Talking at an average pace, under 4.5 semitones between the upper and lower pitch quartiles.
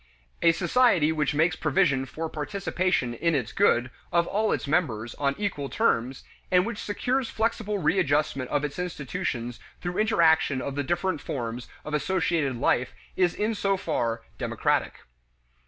No: average, 150 wpm; wide, 5.6 semitones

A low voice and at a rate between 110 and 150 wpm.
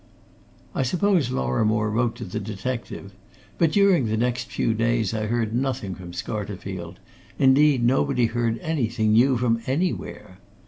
Yes: low, 115 Hz; average, 140 wpm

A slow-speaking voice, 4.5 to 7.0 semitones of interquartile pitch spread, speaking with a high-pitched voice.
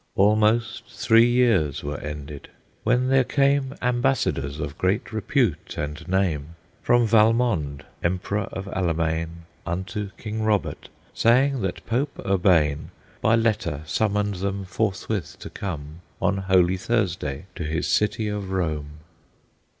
No: slow, 125 wpm; wide, 5.6 semitones; very low, 95 Hz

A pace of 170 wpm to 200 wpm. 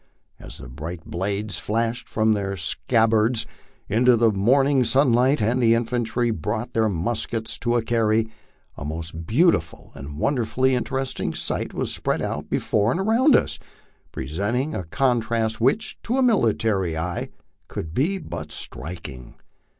No: average, 140 wpm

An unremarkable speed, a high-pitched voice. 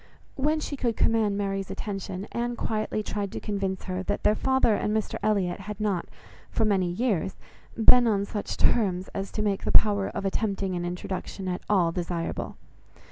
Yes: average, 180 wpm; high, 200 Hz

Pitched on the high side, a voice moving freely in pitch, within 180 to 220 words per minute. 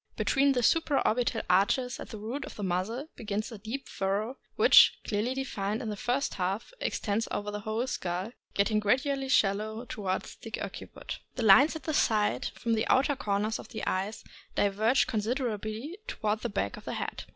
No: high, 220 Hz; average, 3.8 semitones; average, 185 wpm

